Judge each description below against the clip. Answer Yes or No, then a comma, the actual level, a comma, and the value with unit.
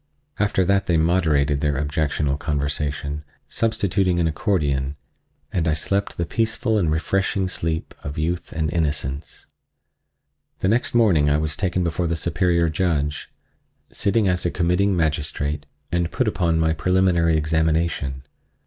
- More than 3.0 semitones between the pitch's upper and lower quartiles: Yes, average, 3.5 semitones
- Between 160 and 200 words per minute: No, average, 140 wpm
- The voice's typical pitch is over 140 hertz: No, very low, 80 Hz